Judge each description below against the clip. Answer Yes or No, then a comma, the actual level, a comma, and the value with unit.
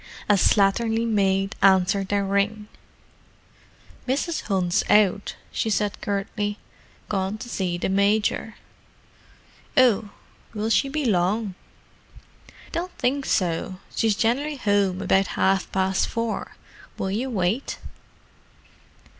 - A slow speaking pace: Yes, slow, 105 wpm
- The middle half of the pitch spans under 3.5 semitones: Yes, average, 2.8 semitones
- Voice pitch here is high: Yes, high, 205 Hz